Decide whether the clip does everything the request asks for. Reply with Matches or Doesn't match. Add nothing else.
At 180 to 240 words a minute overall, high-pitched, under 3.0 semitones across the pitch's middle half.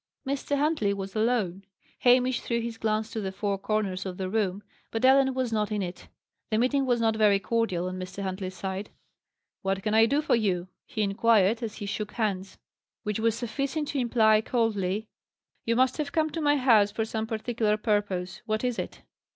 Doesn't match